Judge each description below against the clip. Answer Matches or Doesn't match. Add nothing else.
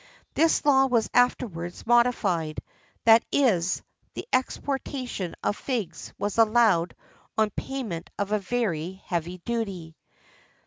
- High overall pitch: Matches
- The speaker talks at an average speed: Doesn't match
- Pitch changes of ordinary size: Doesn't match